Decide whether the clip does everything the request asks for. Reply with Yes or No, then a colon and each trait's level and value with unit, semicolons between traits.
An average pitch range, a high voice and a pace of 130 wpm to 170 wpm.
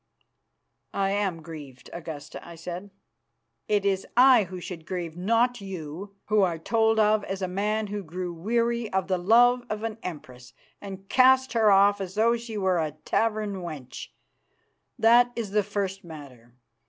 Yes: average, 4.2 semitones; high, 195 Hz; average, 165 wpm